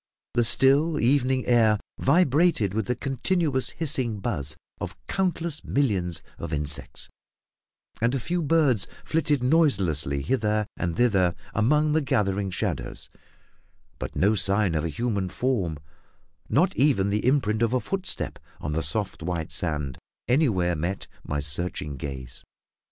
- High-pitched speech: No, low, 110 Hz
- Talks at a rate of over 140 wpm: No, slow, 135 wpm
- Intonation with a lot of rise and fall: Yes, wide, 7.8 semitones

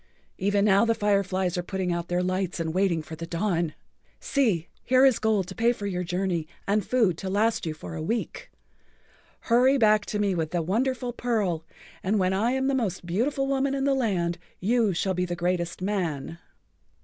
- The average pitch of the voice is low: No, high, 195 Hz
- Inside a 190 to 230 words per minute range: Yes, average, 200 wpm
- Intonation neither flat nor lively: Yes, average, 4.6 semitones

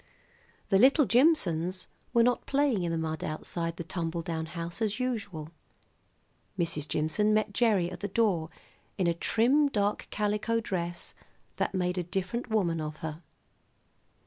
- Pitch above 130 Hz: Yes, medium, 185 Hz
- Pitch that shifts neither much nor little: Yes, average, 5.0 semitones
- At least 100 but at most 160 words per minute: Yes, average, 150 wpm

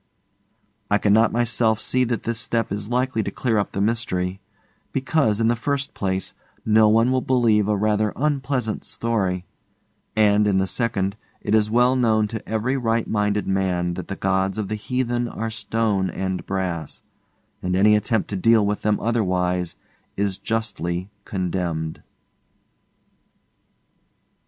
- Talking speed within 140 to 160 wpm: Yes, average, 150 wpm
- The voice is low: Yes, low, 105 Hz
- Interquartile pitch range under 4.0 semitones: Yes, average, 3.2 semitones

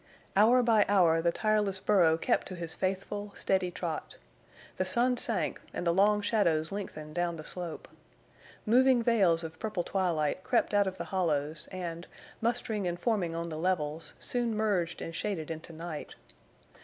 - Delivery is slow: No, average, 165 wpm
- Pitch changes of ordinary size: Yes, average, 4.0 semitones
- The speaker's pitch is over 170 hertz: Yes, medium, 185 Hz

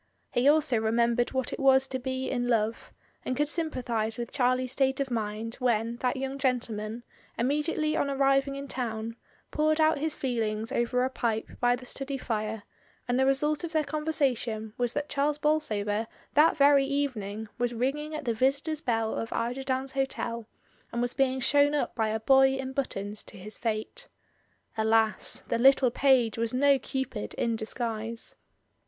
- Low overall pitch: No, very high, 255 Hz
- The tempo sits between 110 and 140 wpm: No, average, 175 wpm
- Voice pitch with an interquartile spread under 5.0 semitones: Yes, average, 3.5 semitones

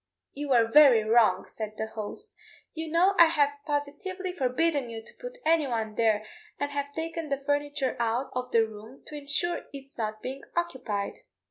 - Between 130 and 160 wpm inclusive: No, average, 170 wpm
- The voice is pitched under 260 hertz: No, very high, 275 Hz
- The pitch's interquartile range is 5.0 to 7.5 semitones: Yes, wide, 5.5 semitones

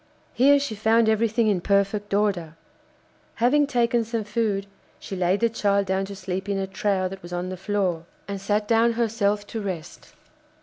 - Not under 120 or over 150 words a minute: No, average, 180 wpm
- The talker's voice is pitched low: No, high, 205 Hz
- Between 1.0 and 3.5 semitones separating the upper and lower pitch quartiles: Yes, average, 2.9 semitones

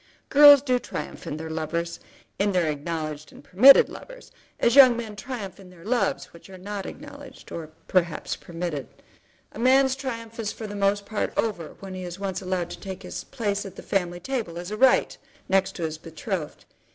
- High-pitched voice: Yes, high, 195 Hz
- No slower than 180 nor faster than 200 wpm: Yes, average, 195 wpm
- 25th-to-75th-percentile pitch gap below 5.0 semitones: No, wide, 5.4 semitones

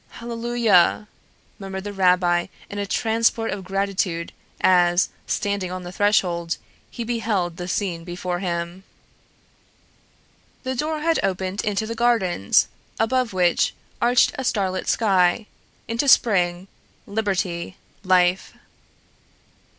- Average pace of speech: No, slow, 110 wpm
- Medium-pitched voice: No, high, 195 Hz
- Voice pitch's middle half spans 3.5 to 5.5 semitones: Yes, average, 4.1 semitones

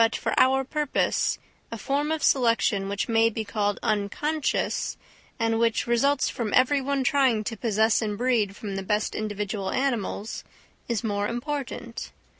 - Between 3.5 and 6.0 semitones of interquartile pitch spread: Yes, average, 4.0 semitones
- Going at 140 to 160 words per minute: Yes, average, 155 wpm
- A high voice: Yes, high, 230 Hz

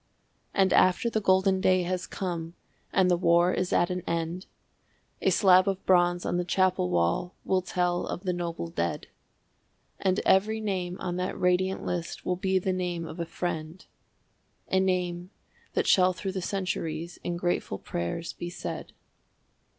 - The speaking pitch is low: No, medium, 180 Hz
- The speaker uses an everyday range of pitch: No, narrow, 1.4 semitones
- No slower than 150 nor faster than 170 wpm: Yes, average, 165 wpm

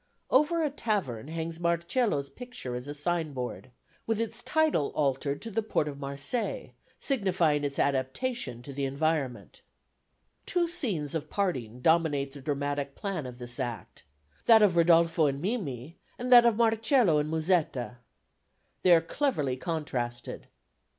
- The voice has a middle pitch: Yes, medium, 160 Hz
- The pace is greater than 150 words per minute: No, average, 145 wpm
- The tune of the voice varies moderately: No, wide, 7.7 semitones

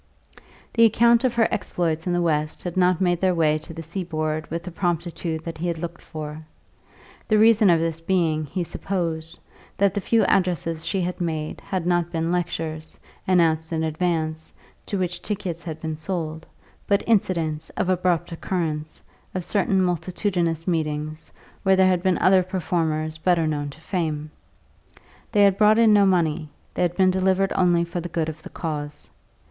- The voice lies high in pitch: No, medium, 170 Hz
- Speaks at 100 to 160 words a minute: No, average, 175 wpm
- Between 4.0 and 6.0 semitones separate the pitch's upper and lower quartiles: No, average, 2.7 semitones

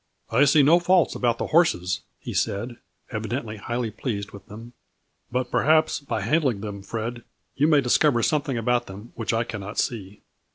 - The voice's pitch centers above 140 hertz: No, low, 120 Hz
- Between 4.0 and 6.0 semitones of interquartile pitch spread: Yes, average, 4.7 semitones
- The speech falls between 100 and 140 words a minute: No, average, 190 wpm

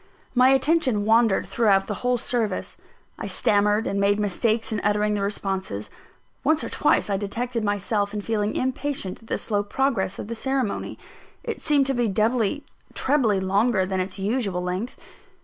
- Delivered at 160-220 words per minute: Yes, average, 165 wpm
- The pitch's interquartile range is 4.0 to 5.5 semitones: No, average, 3.6 semitones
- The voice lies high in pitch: Yes, high, 210 Hz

